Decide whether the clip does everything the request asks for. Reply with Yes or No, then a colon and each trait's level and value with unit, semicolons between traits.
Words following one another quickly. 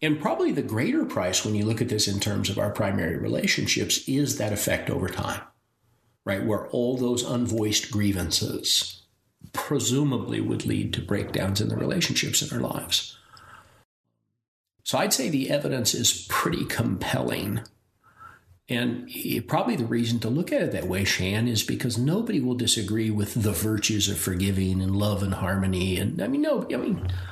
No: average, 170 wpm